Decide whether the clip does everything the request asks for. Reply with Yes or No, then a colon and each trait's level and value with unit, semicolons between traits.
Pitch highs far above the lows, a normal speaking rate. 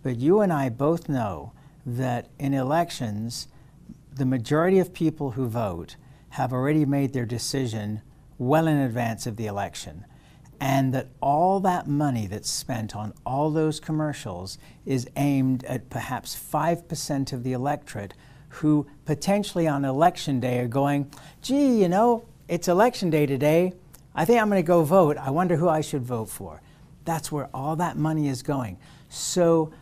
No: average, 3.8 semitones; average, 165 wpm